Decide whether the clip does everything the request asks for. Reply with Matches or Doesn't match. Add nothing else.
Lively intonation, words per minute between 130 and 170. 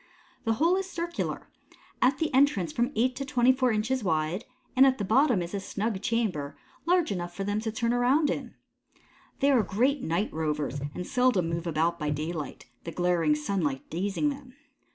Doesn't match